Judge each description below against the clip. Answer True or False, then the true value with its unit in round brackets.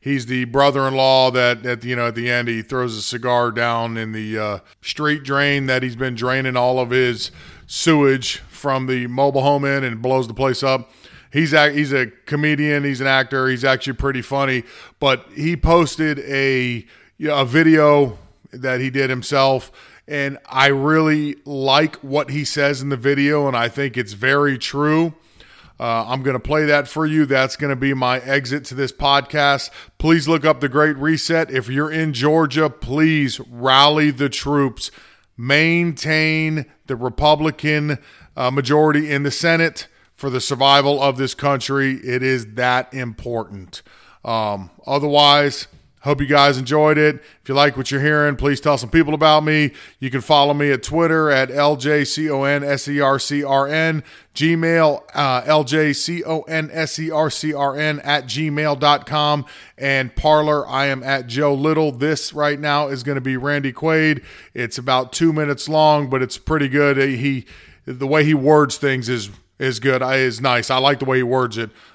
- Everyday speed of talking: True (185 wpm)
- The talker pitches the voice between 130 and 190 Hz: True (140 Hz)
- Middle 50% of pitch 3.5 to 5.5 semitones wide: False (2.6 semitones)